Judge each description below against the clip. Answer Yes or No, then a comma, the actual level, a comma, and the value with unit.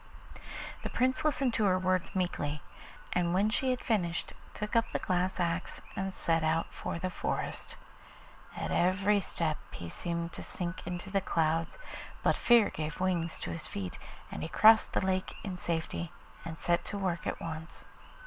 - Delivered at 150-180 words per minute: Yes, average, 175 wpm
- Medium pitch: Yes, medium, 180 Hz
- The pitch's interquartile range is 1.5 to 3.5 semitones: Yes, average, 2.9 semitones